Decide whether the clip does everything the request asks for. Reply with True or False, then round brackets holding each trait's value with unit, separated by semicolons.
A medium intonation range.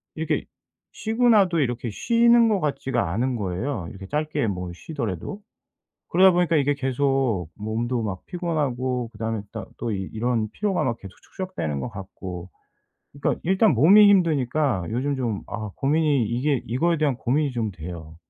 False (6.5 semitones)